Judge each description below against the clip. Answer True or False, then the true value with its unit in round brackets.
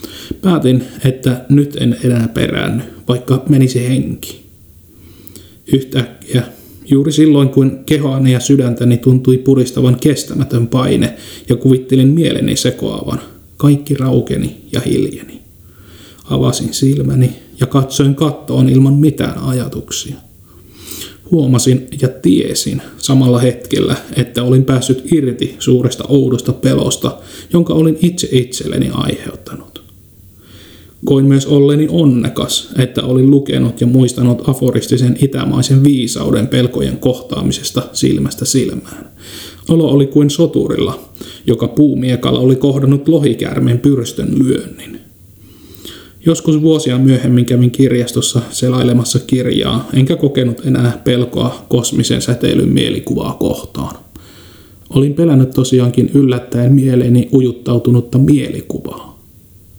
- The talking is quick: False (100 wpm)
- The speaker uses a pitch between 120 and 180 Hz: True (130 Hz)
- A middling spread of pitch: False (2.2 semitones)